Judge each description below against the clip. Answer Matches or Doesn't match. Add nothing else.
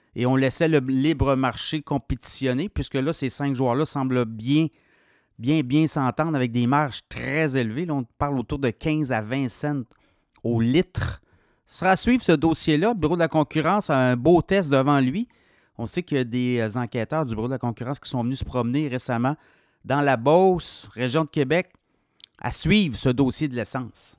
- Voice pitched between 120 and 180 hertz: Matches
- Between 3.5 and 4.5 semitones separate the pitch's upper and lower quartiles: Matches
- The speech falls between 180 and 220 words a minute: Matches